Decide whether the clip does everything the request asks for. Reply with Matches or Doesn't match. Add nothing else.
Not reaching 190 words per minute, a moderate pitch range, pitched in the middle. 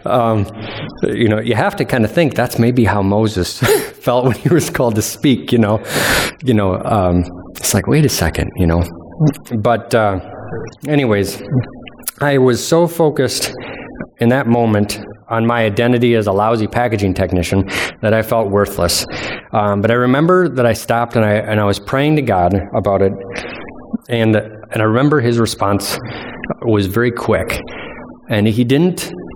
Doesn't match